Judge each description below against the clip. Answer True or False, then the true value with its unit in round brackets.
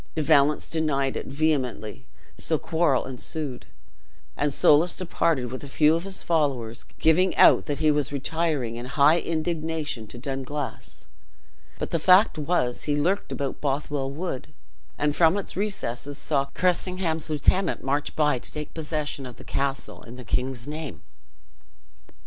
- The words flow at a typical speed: True (155 wpm)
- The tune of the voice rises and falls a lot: False (3.2 semitones)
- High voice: False (150 Hz)